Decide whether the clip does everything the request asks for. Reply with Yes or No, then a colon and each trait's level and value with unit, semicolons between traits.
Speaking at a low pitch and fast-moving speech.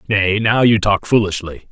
No: low, 105 Hz; average, 175 wpm